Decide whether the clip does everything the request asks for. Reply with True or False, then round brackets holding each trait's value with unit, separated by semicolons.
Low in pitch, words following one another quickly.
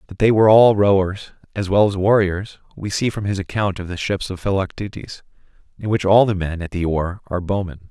True (95 Hz; 220 wpm)